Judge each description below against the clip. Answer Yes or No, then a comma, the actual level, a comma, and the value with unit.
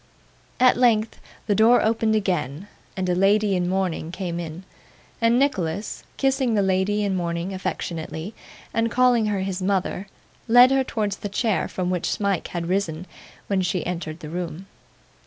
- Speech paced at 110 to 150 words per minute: No, average, 160 wpm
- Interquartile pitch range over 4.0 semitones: No, average, 3.5 semitones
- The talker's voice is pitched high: Yes, high, 195 Hz